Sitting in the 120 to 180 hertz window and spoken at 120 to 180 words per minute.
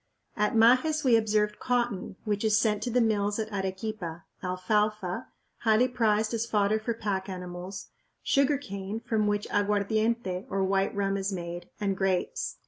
No: high, 210 Hz; average, 155 wpm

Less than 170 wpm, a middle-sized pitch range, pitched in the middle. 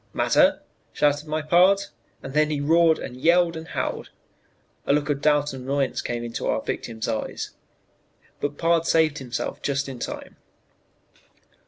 Yes: average, 155 wpm; average, 3.1 semitones; medium, 145 Hz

